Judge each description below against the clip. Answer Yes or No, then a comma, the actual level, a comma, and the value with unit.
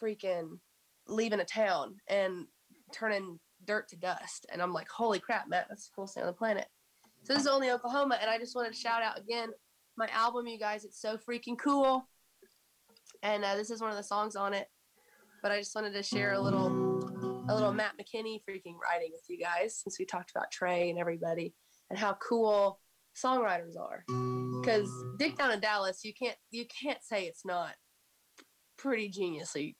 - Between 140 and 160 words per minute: No, average, 195 wpm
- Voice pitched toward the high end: Yes, high, 210 Hz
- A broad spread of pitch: No, average, 4.1 semitones